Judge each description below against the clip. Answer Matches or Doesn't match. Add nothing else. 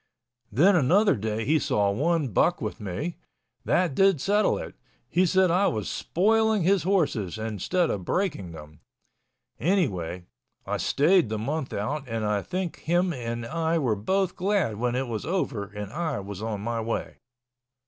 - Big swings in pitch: Matches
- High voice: Doesn't match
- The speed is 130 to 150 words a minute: Doesn't match